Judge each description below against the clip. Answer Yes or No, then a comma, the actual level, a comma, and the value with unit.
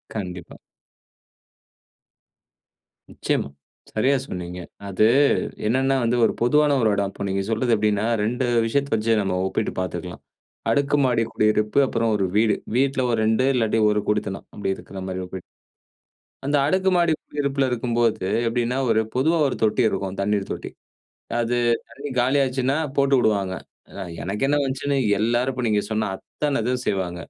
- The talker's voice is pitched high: No, low, 115 Hz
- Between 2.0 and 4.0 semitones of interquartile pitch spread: No, average, 4.5 semitones